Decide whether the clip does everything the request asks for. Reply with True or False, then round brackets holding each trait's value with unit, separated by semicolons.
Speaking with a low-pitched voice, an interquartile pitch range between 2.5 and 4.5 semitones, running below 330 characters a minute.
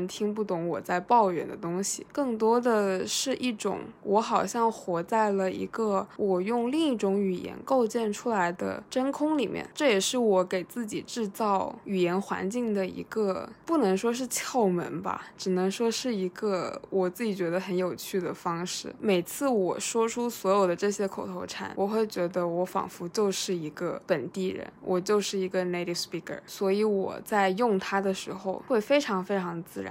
False (195 Hz; 3.8 semitones; 285 characters per minute)